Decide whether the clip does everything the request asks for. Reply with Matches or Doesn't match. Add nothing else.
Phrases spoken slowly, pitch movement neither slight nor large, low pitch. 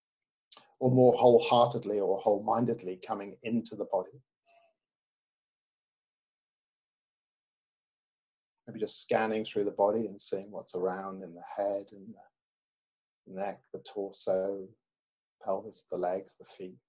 Matches